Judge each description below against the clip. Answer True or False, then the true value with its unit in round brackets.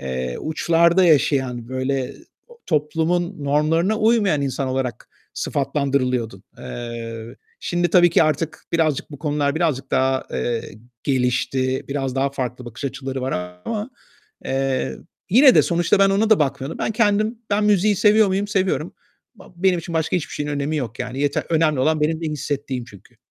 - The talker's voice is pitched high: False (145 Hz)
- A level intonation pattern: False (4.9 semitones)